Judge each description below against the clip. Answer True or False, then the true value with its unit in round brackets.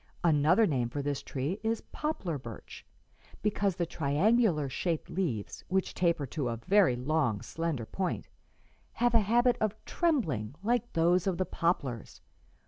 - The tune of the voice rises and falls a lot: True (6.8 semitones)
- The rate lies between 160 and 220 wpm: False (145 wpm)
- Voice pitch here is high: False (170 Hz)